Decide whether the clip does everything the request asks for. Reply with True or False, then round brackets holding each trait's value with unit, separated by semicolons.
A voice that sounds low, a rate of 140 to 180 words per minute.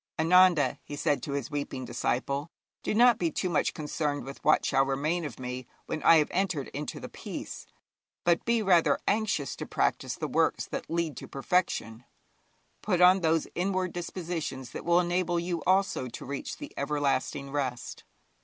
False (160 Hz; 175 wpm)